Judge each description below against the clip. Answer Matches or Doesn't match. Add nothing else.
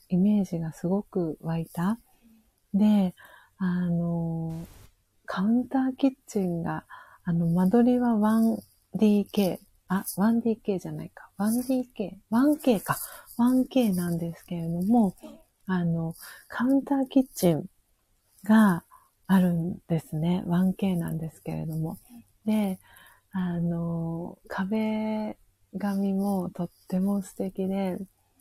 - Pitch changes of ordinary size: Matches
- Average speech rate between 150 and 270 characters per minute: Matches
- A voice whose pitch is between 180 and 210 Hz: Matches